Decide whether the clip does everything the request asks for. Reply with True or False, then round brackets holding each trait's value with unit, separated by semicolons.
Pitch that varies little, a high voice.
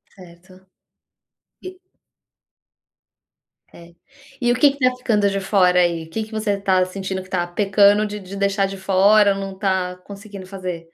True (2.1 semitones; 195 Hz)